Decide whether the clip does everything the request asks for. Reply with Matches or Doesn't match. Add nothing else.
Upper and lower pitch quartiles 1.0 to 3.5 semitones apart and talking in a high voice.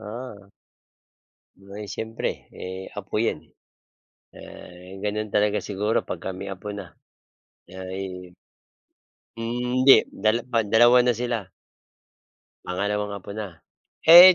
Doesn't match